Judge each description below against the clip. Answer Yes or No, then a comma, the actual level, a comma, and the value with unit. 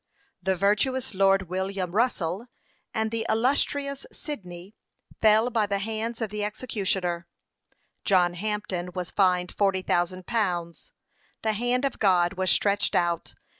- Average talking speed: No, slow, 130 wpm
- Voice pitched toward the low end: No, high, 200 Hz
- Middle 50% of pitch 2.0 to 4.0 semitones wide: Yes, average, 3.6 semitones